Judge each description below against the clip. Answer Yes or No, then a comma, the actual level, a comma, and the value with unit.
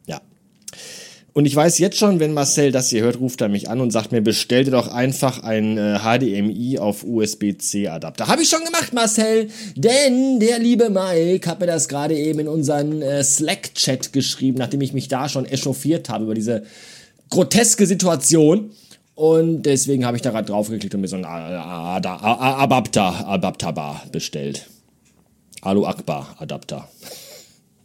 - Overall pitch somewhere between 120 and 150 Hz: Yes, low, 135 Hz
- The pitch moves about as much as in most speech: No, wide, 7.0 semitones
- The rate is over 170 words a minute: No, average, 155 wpm